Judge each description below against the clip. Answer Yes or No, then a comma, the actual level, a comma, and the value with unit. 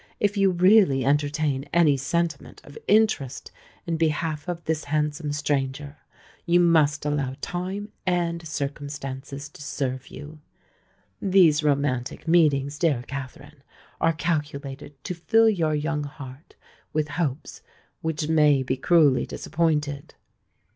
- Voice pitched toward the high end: No, medium, 150 Hz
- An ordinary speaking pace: No, slow, 120 wpm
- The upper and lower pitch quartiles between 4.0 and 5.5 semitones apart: No, average, 3.0 semitones